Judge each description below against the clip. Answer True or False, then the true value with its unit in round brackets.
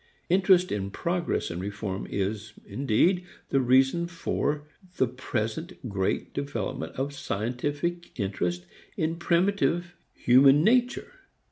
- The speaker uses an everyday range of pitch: False (8.2 semitones)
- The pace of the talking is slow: True (110 wpm)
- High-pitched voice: False (135 Hz)